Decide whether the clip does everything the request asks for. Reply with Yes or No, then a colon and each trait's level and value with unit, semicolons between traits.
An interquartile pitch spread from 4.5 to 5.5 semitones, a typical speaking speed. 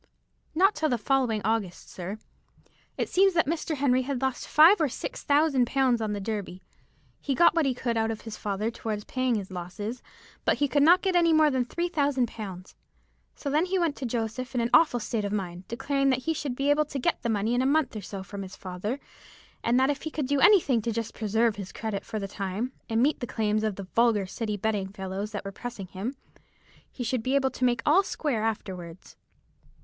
No: average, 5.2 semitones; fast, 225 wpm